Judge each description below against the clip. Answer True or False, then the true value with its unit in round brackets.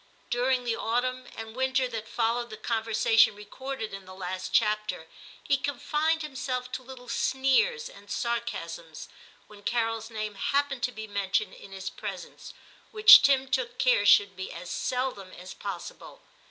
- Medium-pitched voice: False (235 Hz)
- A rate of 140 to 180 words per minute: True (155 wpm)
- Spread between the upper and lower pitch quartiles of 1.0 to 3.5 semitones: False (4.2 semitones)